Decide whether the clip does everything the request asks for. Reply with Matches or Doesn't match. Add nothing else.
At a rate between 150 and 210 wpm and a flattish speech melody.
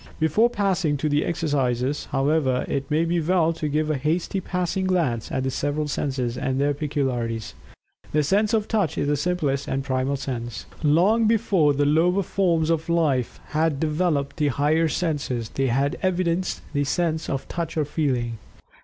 Doesn't match